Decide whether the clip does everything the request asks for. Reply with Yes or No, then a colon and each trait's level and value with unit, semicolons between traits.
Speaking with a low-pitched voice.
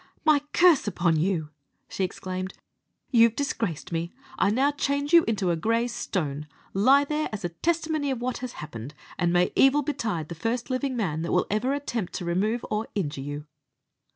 No: high, 215 Hz